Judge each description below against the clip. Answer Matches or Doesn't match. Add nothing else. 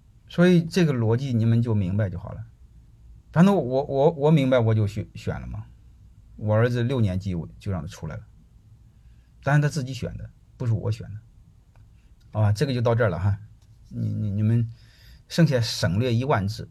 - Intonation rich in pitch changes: Doesn't match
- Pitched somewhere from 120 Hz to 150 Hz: Doesn't match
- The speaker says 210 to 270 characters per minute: Matches